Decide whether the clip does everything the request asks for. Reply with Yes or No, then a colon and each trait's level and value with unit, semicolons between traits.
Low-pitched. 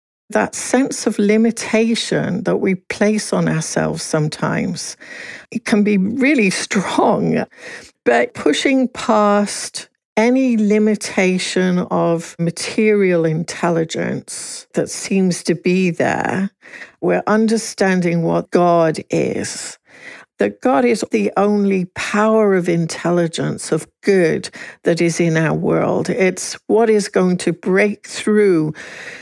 No: high, 195 Hz